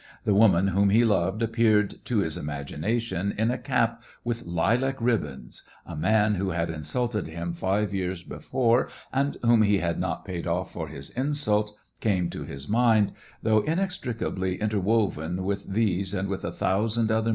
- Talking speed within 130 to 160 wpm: No, average, 175 wpm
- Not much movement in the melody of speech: No, average, 4.3 semitones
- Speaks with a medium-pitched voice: No, low, 105 Hz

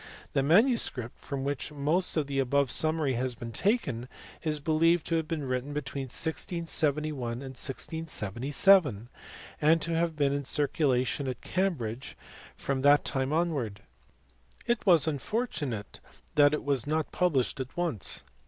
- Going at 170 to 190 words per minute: No, average, 145 wpm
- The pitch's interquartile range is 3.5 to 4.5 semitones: Yes, average, 3.8 semitones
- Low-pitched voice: No, medium, 145 Hz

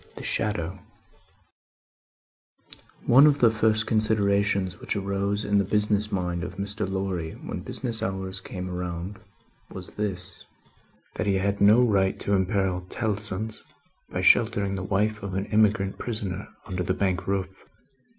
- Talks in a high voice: No, low, 100 Hz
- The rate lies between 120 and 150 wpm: Yes, average, 140 wpm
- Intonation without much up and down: Yes, narrow, 2.1 semitones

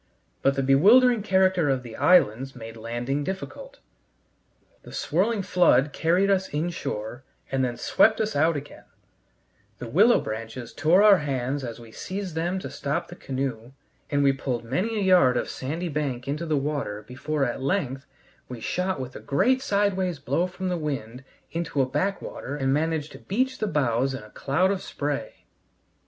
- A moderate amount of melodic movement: No, wide, 6.1 semitones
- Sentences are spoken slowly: No, average, 175 wpm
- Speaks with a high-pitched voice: No, medium, 145 Hz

